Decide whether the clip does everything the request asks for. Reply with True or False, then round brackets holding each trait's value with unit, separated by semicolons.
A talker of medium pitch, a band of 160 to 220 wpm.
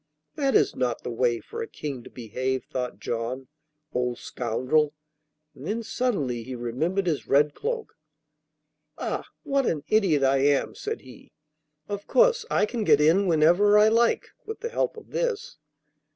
True (155 Hz; 165 wpm)